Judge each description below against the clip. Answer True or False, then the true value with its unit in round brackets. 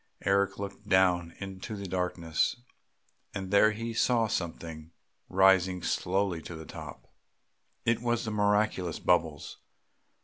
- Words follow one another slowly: True (125 wpm)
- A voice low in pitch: True (95 Hz)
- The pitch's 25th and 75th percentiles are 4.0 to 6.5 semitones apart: False (2.8 semitones)